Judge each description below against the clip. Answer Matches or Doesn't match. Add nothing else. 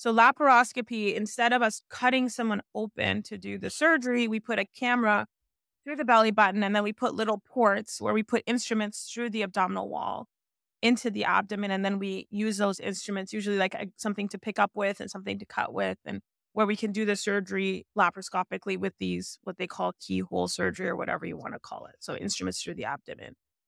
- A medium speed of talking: Doesn't match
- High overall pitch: Matches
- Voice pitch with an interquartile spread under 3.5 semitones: Matches